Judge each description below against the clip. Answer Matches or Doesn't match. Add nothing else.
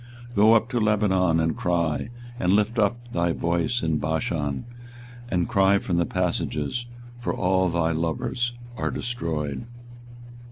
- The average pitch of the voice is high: Doesn't match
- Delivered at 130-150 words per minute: Matches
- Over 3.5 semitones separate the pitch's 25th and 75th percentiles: Matches